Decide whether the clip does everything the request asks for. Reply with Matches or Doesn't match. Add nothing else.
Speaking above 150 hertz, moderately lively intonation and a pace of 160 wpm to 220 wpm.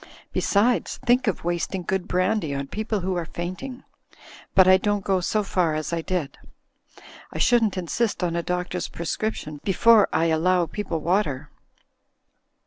Doesn't match